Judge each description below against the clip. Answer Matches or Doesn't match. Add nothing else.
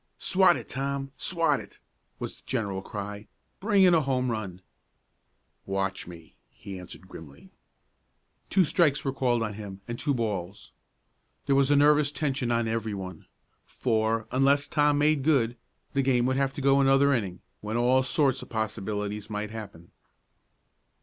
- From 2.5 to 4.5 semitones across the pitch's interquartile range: Doesn't match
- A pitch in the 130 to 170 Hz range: Doesn't match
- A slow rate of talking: Doesn't match